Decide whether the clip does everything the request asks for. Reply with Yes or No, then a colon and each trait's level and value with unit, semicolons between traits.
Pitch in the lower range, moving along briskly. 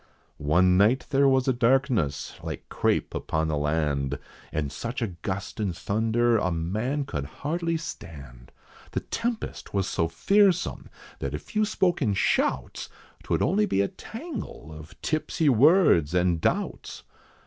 No: low, 105 Hz; average, 150 wpm